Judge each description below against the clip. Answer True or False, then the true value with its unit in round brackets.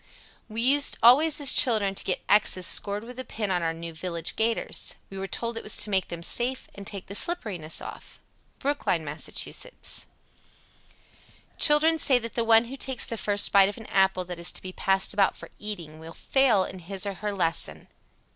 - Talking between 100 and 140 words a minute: False (205 wpm)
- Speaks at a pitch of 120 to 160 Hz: False (205 Hz)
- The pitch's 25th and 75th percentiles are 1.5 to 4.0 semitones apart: False (4.4 semitones)